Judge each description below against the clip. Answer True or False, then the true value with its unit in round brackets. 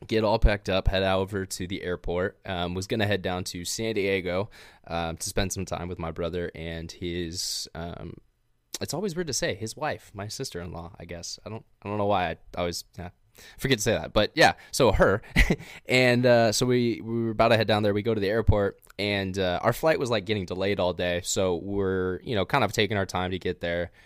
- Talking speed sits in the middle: False (235 wpm)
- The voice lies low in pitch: True (95 Hz)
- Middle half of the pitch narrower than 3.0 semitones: False (3.8 semitones)